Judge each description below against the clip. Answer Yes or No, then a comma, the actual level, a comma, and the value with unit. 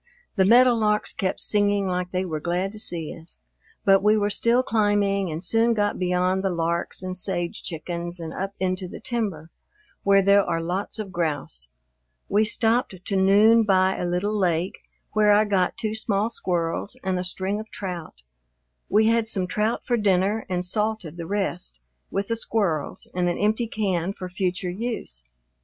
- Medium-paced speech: Yes, average, 175 wpm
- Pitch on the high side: Yes, high, 195 Hz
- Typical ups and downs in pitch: Yes, average, 3.0 semitones